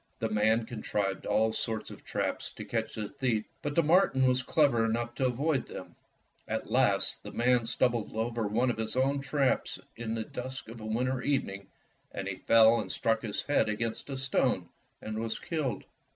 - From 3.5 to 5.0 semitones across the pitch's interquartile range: No, average, 2.9 semitones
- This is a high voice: No, low, 115 Hz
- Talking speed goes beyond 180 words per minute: Yes, average, 190 wpm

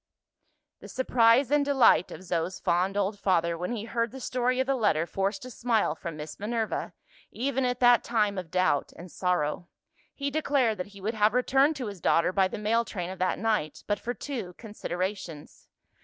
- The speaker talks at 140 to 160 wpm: No, average, 195 wpm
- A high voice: Yes, high, 210 Hz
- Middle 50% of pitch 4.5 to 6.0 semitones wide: Yes, average, 5.1 semitones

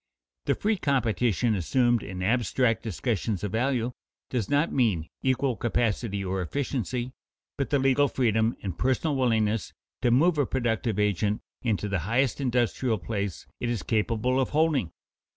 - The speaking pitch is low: Yes, low, 120 Hz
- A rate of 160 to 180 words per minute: No, average, 150 wpm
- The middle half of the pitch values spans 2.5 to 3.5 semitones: No, average, 3.9 semitones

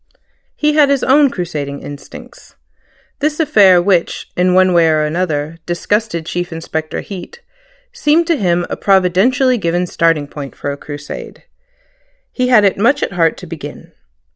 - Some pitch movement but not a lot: No, wide, 7.5 semitones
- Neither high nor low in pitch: Yes, medium, 180 Hz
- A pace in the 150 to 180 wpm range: Yes, average, 155 wpm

